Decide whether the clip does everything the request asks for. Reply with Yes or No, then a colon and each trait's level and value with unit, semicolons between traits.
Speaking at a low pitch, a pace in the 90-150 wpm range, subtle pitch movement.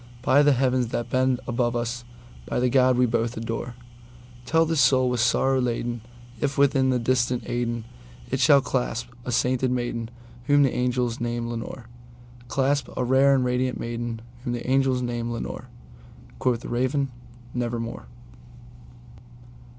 Yes: low, 125 Hz; average, 140 wpm; narrow, 1.5 semitones